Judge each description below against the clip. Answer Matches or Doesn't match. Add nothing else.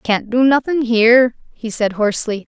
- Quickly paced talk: Doesn't match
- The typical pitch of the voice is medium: Doesn't match